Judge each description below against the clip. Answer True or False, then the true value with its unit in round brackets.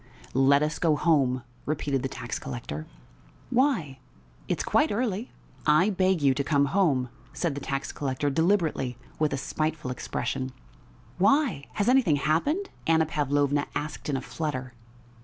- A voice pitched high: False (150 Hz)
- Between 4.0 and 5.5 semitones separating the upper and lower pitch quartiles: True (4.5 semitones)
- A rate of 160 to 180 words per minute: False (145 wpm)